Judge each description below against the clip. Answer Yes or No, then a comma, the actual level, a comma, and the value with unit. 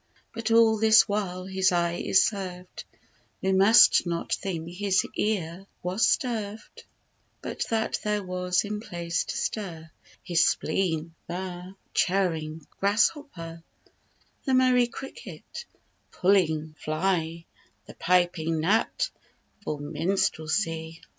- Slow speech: Yes, slow, 110 wpm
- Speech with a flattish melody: No, average, 3.9 semitones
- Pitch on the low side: No, medium, 185 Hz